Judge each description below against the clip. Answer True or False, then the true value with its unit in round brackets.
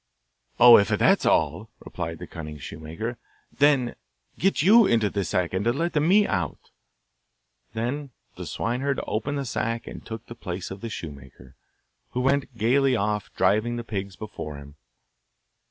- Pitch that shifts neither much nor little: False (6.3 semitones)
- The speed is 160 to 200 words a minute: False (150 wpm)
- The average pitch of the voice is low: True (115 Hz)